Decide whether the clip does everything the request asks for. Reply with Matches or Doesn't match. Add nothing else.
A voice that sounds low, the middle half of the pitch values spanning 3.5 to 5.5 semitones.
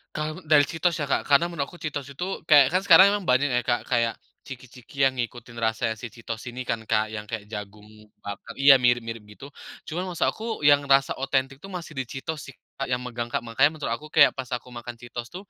Matches